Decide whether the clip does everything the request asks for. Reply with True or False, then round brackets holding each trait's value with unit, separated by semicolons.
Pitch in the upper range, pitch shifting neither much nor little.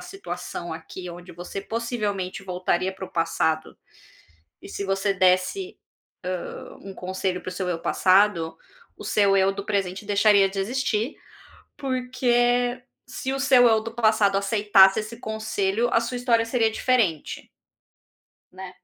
True (200 Hz; 3.7 semitones)